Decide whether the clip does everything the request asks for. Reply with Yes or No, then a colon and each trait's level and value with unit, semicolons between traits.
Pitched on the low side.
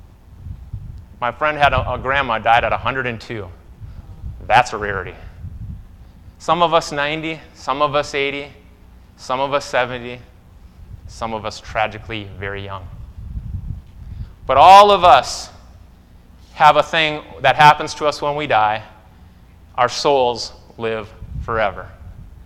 Yes: low, 110 Hz